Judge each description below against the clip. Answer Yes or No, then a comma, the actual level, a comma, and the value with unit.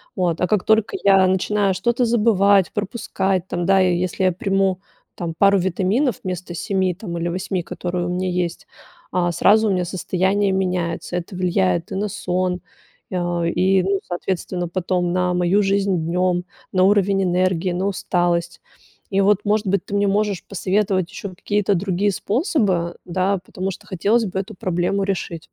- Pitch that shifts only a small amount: Yes, narrow, 1.9 semitones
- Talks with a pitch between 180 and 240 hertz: Yes, medium, 185 Hz